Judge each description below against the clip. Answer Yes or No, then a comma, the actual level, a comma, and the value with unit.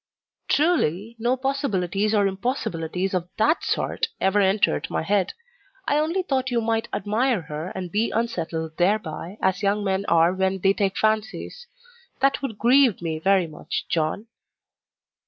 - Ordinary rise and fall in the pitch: Yes, average, 4.6 semitones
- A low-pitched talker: No, high, 200 Hz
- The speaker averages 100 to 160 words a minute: Yes, average, 150 wpm